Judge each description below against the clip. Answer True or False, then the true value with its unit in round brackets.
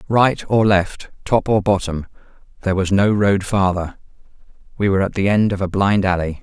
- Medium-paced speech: True (185 wpm)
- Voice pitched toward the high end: False (100 Hz)